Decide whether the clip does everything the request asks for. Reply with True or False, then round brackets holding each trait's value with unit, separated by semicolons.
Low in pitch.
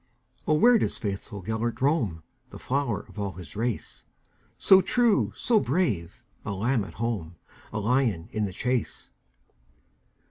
True (115 Hz)